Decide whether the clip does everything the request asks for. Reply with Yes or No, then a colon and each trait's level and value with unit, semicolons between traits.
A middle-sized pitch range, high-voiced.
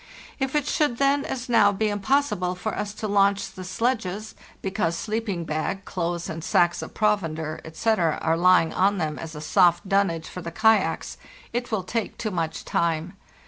Yes: average, 4.5 semitones; high, 195 Hz